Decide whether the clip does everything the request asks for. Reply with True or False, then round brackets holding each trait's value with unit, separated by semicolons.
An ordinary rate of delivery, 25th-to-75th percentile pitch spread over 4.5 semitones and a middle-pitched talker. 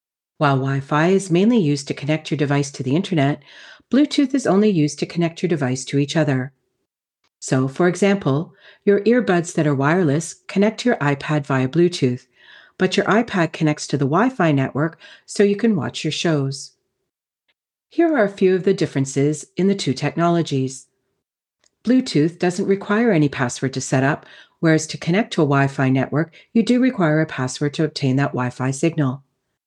True (175 wpm; 5.6 semitones; 155 Hz)